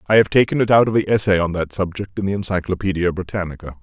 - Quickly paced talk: Yes, fast, 235 wpm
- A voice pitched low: Yes, very low, 95 Hz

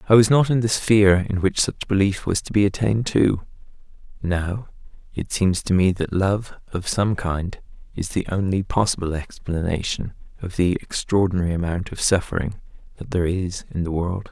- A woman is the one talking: No, male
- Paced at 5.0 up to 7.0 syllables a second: Yes, 5.1 syllables/s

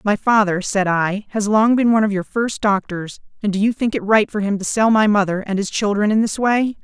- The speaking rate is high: Yes, fast, 265 wpm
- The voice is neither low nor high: No, high, 205 Hz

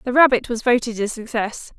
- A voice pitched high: Yes, high, 235 Hz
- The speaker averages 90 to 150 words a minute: No, average, 200 wpm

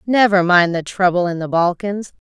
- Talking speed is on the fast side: No, average, 180 wpm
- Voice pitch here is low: No, medium, 185 Hz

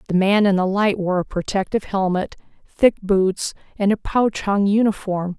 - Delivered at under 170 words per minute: No, average, 180 wpm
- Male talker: No, female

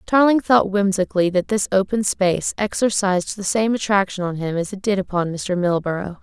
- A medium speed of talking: Yes, average, 185 wpm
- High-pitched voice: Yes, high, 195 Hz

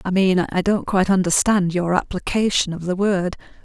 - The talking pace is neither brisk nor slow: Yes, average, 180 wpm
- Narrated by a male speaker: No, female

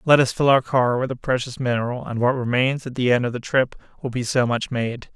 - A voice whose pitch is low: Yes, low, 125 Hz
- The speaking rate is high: Yes, fast, 270 wpm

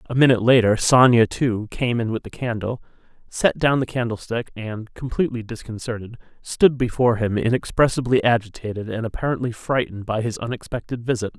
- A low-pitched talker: Yes, low, 115 Hz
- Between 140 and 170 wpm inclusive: Yes, average, 155 wpm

